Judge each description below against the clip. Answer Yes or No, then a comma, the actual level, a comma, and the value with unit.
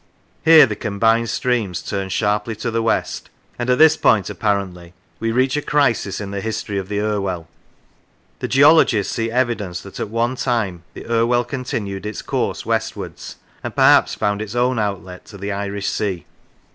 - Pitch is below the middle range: Yes, low, 110 Hz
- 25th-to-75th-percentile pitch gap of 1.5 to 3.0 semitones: No, average, 3.4 semitones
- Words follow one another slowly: No, average, 170 wpm